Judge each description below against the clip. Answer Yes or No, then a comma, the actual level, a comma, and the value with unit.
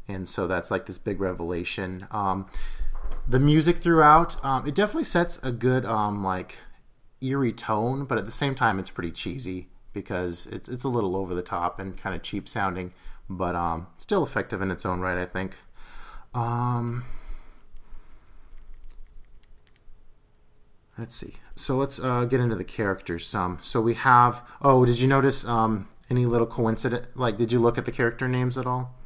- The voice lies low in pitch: Yes, low, 110 Hz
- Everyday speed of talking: Yes, average, 175 wpm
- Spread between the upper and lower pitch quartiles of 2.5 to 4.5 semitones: No, wide, 5.4 semitones